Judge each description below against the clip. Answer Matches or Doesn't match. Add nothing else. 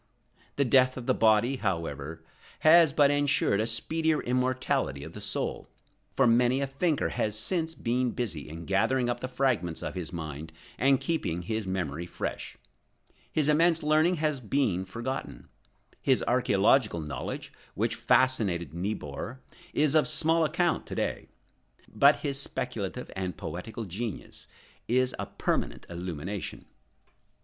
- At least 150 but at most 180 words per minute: Doesn't match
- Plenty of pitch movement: Matches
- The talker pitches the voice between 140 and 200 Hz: Doesn't match